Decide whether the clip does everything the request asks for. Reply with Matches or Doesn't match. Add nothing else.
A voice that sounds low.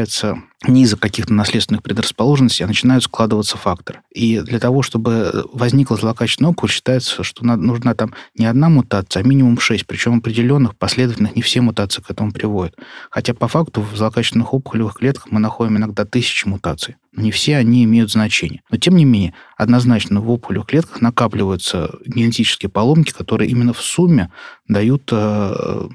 Matches